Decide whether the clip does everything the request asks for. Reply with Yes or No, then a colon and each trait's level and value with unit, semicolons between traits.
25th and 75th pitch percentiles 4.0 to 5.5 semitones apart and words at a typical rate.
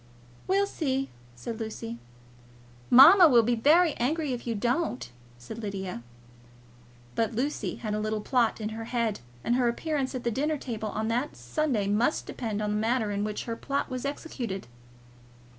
Yes: average, 4.3 semitones; average, 170 wpm